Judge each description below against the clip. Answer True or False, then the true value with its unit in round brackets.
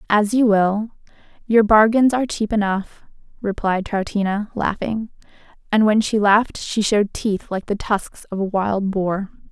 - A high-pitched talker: True (210 Hz)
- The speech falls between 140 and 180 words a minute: True (160 wpm)